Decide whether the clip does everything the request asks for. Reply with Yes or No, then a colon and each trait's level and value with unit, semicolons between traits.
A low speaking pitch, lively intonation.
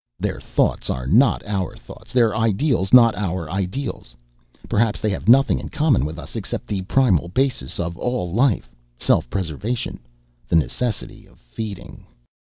Yes: low, 105 Hz; wide, 6.1 semitones